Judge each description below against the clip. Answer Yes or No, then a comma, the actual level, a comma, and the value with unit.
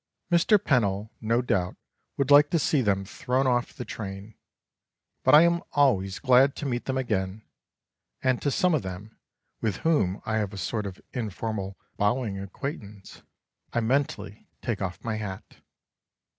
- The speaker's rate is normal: Yes, average, 155 wpm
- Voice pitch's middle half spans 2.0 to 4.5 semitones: No, average, 5.3 semitones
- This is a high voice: No, low, 115 Hz